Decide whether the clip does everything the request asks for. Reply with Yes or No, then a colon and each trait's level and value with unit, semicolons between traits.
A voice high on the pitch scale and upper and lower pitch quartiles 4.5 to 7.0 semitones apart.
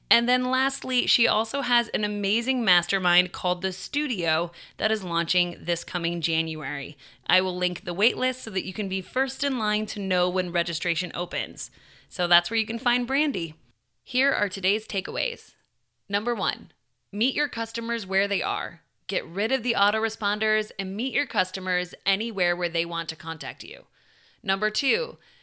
Yes: high, 200 Hz; average, 5.1 semitones